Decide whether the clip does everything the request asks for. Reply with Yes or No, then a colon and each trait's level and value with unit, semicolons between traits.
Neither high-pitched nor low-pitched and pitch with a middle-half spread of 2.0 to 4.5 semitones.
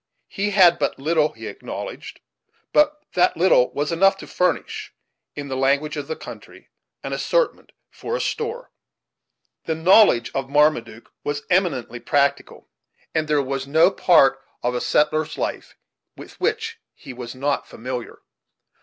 No: medium, 150 Hz; average, 5.1 semitones